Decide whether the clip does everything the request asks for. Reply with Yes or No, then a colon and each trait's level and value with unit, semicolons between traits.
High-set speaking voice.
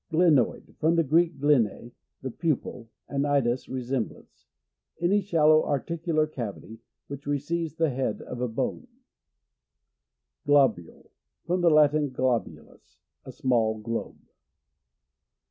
No: medium, 145 Hz